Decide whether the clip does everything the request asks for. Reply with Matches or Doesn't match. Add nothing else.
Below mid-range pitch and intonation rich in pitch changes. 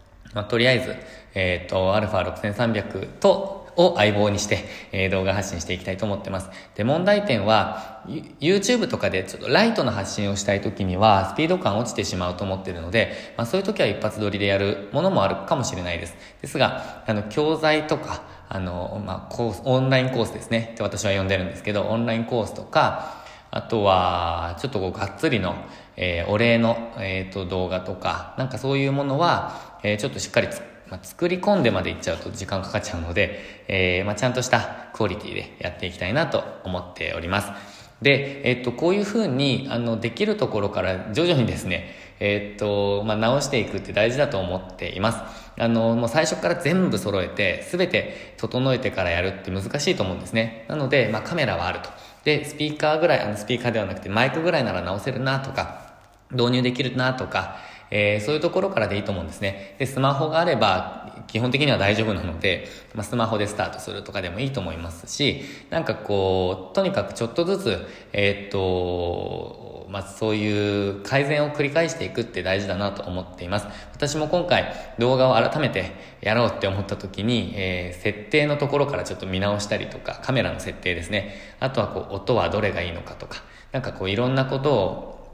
Doesn't match